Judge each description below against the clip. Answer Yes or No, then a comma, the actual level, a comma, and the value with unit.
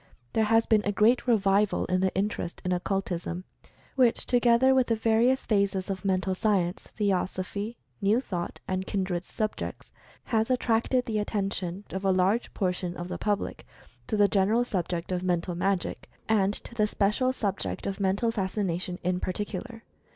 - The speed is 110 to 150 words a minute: No, average, 165 wpm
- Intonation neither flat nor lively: Yes, average, 3.2 semitones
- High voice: Yes, high, 200 Hz